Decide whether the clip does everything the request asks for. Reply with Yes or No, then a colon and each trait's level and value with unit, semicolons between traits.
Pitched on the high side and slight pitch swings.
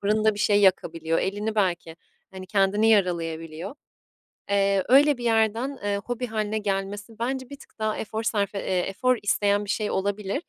Yes: high, 205 Hz; narrow, 2.3 semitones